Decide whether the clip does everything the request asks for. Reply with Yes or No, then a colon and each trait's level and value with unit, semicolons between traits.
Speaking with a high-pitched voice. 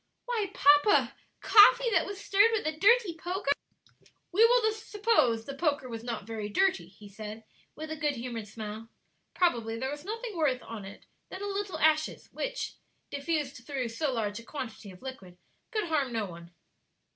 Yes: very high, 290 Hz